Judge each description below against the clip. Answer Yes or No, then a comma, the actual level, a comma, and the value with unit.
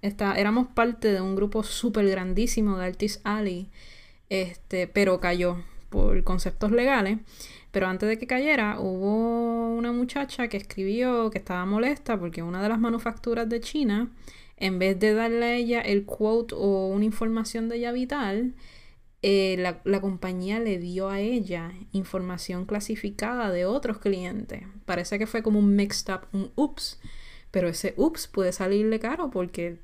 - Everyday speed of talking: Yes, average, 160 wpm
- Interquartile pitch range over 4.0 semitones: No, average, 3.5 semitones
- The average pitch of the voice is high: Yes, high, 205 Hz